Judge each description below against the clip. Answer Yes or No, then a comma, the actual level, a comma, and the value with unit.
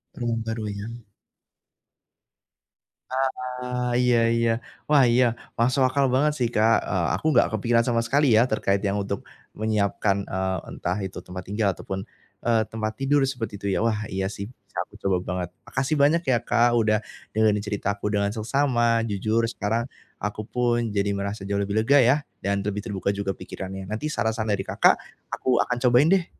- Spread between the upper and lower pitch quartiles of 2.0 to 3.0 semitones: No, average, 3.6 semitones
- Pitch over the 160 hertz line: No, low, 110 Hz